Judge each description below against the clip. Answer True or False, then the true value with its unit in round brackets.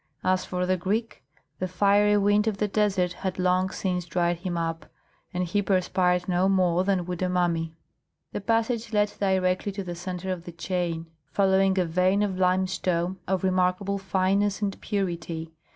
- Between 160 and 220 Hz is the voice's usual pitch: True (185 Hz)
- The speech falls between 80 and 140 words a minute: False (170 wpm)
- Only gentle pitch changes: True (1.8 semitones)